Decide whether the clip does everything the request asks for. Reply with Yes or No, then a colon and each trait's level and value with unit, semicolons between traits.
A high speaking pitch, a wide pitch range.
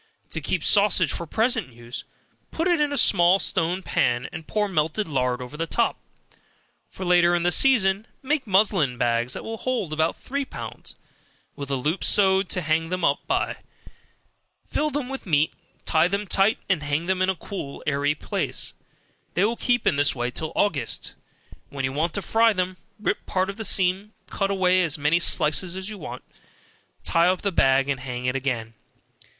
No: medium, 180 Hz; wide, 5.7 semitones